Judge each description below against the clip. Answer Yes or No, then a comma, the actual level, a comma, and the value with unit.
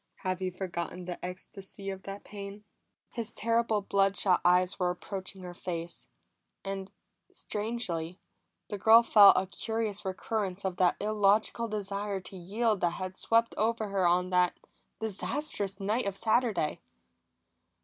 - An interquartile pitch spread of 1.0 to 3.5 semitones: Yes, average, 2.7 semitones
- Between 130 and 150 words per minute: Yes, average, 140 wpm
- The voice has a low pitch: No, high, 195 Hz